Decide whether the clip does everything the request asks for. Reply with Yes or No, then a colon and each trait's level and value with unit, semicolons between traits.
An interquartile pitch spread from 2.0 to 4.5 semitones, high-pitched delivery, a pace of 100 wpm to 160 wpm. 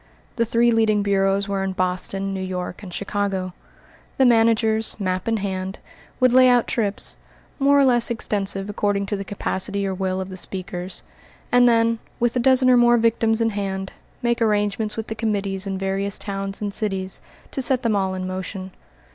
No: average, 3.0 semitones; high, 205 Hz; average, 185 wpm